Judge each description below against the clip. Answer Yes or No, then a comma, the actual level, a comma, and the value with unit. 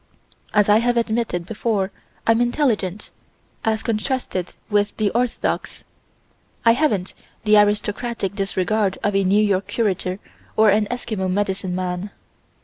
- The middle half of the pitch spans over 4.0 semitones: No, average, 2.8 semitones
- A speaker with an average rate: No, slow, 130 wpm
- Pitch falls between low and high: No, high, 210 Hz